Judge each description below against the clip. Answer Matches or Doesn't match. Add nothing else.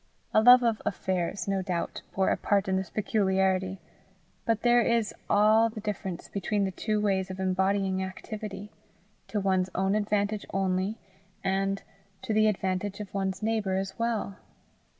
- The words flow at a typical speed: Matches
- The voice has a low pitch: Doesn't match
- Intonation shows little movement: Matches